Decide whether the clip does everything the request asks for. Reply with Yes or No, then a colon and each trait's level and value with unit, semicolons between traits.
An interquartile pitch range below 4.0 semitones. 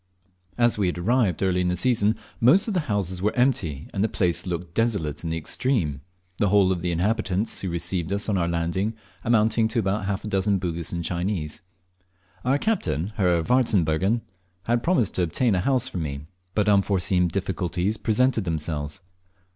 No: average, 4.4 semitones